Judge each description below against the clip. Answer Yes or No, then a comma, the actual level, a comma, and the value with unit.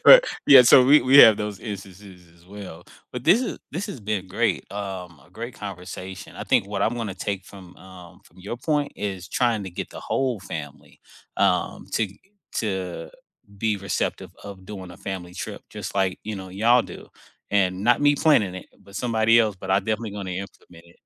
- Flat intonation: No, average, 3.7 semitones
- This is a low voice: Yes, low, 100 Hz